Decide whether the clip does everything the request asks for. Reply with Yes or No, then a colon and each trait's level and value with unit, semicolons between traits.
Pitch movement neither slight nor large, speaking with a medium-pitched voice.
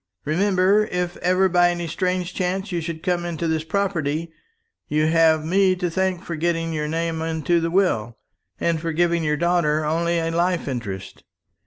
No: narrow, 2.0 semitones; medium, 170 Hz